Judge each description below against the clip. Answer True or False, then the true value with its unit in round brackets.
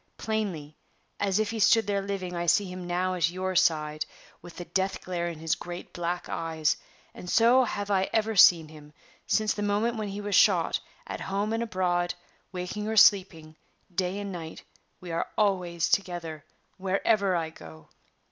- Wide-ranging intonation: False (3.2 semitones)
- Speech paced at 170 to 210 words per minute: True (175 wpm)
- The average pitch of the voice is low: False (185 Hz)